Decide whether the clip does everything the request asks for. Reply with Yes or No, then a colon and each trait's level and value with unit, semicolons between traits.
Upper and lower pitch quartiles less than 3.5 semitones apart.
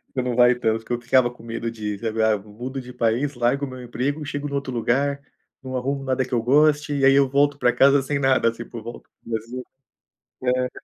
Yes: average, 2.9 semitones